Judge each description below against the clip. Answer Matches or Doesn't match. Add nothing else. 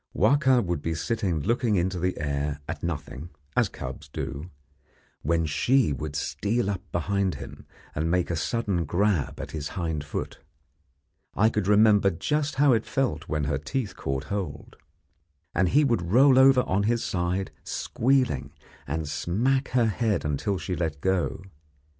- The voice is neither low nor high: Doesn't match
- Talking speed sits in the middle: Matches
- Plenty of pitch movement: Matches